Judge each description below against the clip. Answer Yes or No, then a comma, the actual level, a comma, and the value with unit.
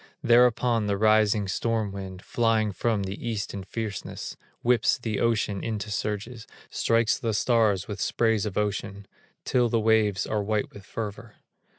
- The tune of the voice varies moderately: No, narrow, 2.1 semitones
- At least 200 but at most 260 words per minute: No, average, 155 wpm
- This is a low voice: Yes, low, 110 Hz